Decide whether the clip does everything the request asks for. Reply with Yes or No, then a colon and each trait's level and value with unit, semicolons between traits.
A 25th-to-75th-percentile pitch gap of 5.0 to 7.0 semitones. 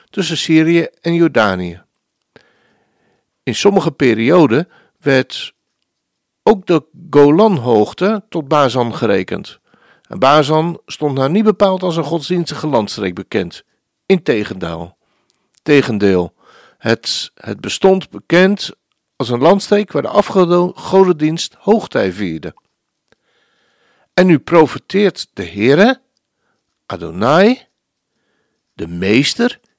Yes: wide, 5.6 semitones